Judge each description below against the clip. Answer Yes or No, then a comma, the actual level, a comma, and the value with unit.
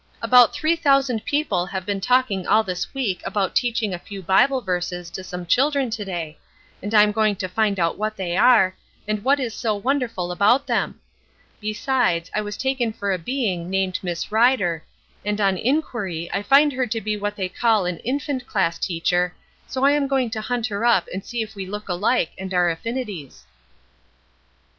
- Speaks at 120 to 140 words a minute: No, average, 195 wpm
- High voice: Yes, high, 210 Hz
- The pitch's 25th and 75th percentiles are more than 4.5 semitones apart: Yes, average, 5.1 semitones